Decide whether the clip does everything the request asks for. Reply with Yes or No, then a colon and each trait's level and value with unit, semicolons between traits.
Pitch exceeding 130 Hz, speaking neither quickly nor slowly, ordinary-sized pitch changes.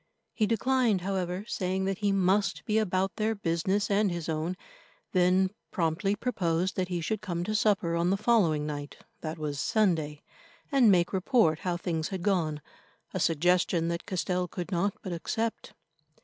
Yes: medium, 185 Hz; average, 160 wpm; average, 3.4 semitones